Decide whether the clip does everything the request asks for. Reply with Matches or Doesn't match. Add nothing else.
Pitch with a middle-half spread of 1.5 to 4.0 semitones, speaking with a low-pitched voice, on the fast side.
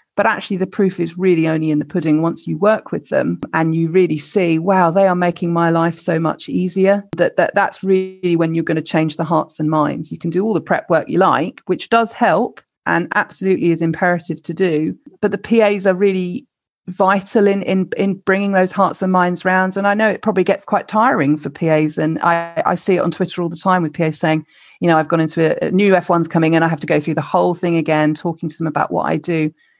Doesn't match